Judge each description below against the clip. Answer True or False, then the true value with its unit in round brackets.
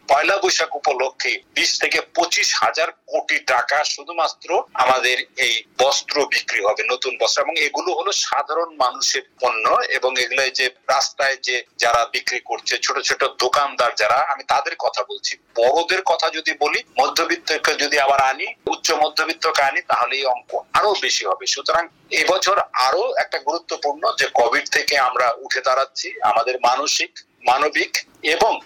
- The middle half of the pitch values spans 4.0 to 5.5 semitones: True (5.1 semitones)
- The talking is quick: True (150 wpm)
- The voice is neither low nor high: True (160 Hz)